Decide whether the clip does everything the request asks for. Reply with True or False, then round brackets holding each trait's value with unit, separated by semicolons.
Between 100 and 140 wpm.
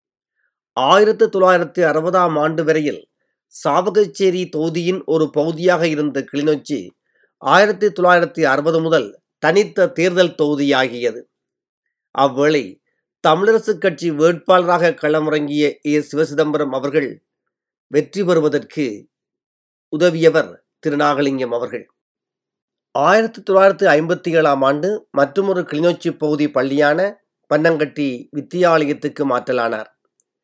False (85 wpm)